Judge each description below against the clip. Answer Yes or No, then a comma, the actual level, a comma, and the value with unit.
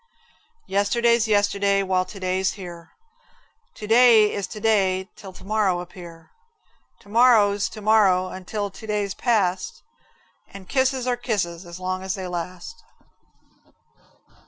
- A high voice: Yes, high, 200 Hz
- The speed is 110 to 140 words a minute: Yes, slow, 135 wpm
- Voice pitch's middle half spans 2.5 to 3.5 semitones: Yes, average, 2.8 semitones